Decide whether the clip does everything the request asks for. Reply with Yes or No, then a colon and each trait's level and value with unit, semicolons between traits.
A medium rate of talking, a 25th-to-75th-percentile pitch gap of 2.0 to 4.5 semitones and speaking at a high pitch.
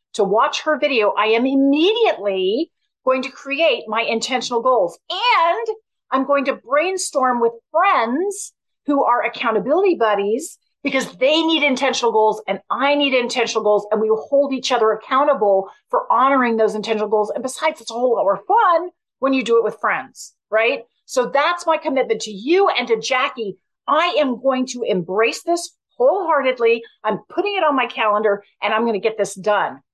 No: average, 180 wpm; wide, 5.6 semitones; very high, 260 Hz